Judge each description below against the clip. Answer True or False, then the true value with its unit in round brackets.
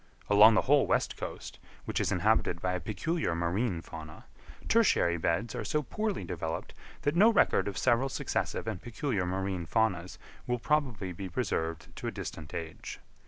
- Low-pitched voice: True (100 Hz)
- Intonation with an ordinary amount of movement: False (7.0 semitones)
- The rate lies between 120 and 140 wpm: False (165 wpm)